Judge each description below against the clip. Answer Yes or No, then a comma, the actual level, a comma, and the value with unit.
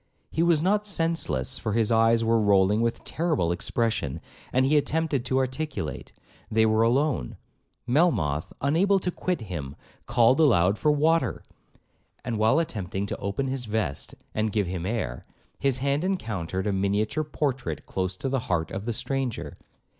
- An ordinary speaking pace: Yes, average, 160 wpm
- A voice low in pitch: Yes, low, 115 Hz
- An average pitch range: No, wide, 6.8 semitones